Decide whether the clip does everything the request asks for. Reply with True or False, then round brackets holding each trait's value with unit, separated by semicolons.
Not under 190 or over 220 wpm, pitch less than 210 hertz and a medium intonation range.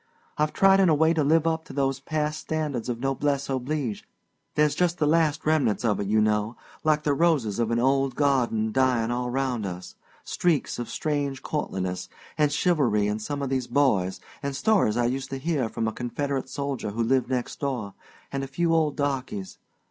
True (195 wpm; 135 Hz; 4.3 semitones)